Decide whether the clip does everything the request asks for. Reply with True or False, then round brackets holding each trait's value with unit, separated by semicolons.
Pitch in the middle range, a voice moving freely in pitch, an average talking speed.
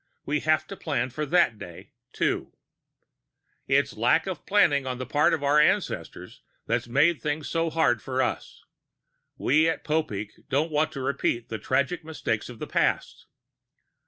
False (145 Hz; 3.8 semitones; 165 wpm)